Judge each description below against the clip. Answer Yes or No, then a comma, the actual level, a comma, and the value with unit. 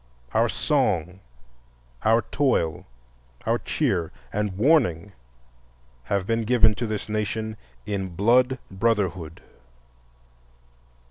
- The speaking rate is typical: No, slow, 90 wpm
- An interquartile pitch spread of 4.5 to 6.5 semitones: No, average, 3.5 semitones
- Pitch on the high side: No, low, 105 Hz